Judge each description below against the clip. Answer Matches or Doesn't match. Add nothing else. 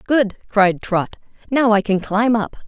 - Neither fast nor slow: Matches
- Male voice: Doesn't match